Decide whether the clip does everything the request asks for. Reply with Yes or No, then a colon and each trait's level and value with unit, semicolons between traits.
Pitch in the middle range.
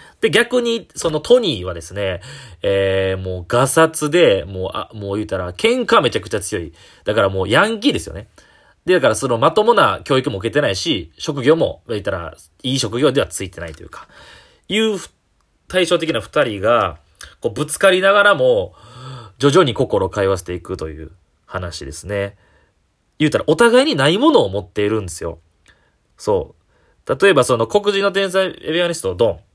No: low, 120 Hz